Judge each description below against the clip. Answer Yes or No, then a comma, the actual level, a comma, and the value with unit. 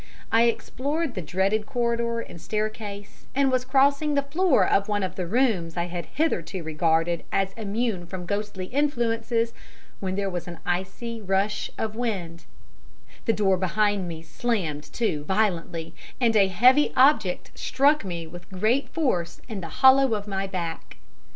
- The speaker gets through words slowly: No, average, 155 wpm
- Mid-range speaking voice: No, high, 205 Hz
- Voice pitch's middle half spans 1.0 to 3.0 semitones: No, average, 5.0 semitones